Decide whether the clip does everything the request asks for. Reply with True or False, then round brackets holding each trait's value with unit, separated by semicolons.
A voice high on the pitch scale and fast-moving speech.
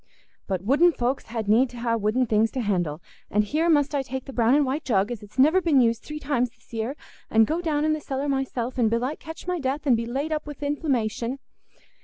True (260 Hz; 235 wpm)